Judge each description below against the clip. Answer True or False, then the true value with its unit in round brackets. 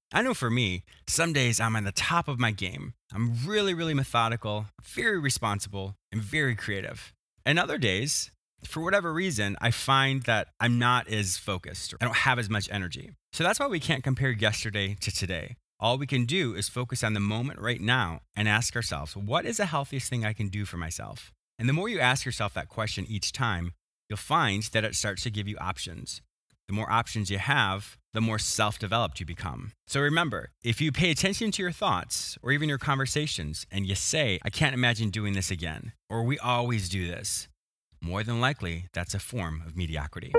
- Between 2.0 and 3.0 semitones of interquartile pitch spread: False (4.6 semitones)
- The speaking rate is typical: False (210 wpm)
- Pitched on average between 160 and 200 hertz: False (110 Hz)